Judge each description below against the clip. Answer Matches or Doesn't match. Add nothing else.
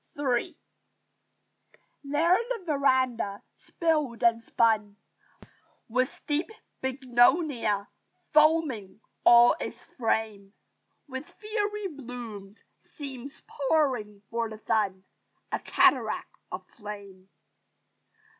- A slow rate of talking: Matches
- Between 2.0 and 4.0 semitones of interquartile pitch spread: Doesn't match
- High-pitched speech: Matches